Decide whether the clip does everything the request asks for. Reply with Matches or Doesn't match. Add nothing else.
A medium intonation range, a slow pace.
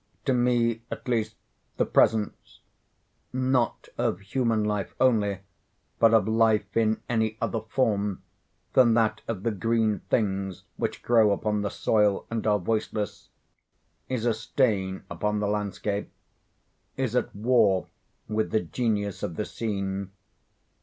Doesn't match